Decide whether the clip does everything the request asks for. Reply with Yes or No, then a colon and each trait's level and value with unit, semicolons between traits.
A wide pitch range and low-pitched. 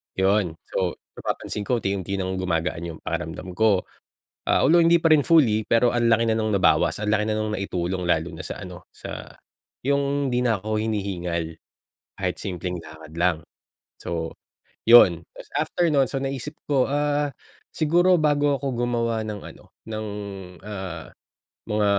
Yes: wide, 6.9 semitones; low, 110 Hz